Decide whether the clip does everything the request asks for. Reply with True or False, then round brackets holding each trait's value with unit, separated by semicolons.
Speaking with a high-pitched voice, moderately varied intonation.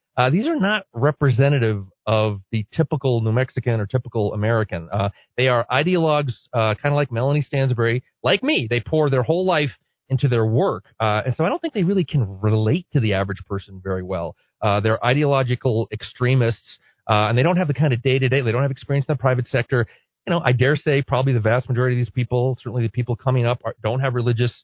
False (125 Hz; 4.0 semitones)